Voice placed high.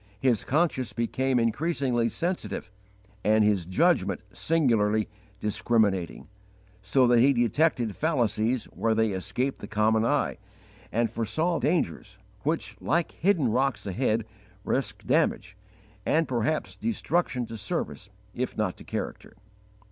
No: low, 120 Hz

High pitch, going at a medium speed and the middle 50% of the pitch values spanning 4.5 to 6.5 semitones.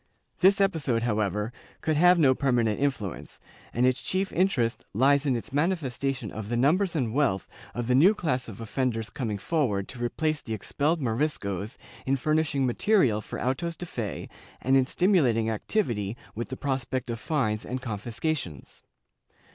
No: low, 130 Hz; average, 160 wpm; wide, 5.4 semitones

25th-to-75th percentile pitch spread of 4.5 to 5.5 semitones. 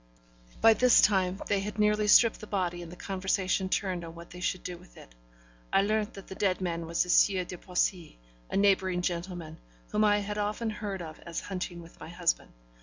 No: average, 2.9 semitones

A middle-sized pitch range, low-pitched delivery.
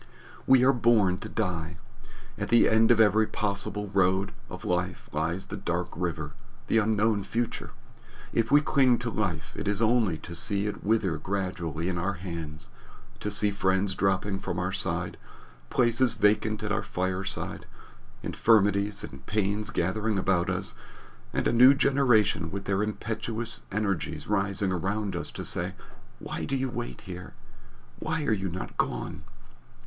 Yes: average, 3.3 semitones; low, 100 Hz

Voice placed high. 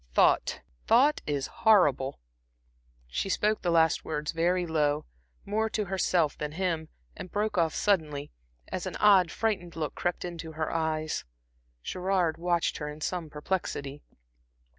No: medium, 170 Hz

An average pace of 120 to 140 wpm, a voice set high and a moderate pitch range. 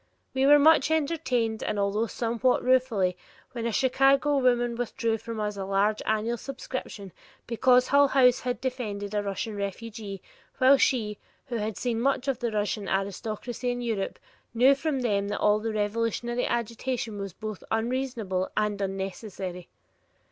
No: average, 150 wpm; high, 230 Hz; average, 3.6 semitones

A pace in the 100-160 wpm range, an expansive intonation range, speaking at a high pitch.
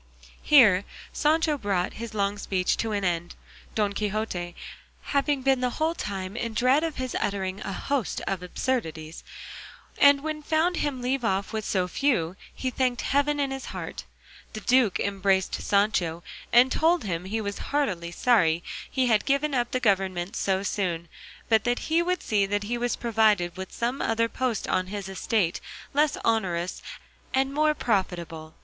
No: average, 170 wpm; wide, 5.8 semitones; high, 220 Hz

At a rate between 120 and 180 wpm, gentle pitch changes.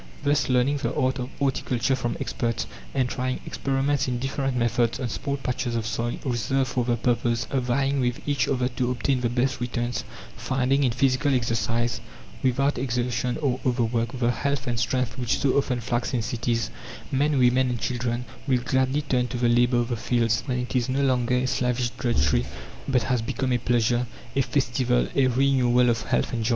No: average, 190 wpm; narrow, 1.7 semitones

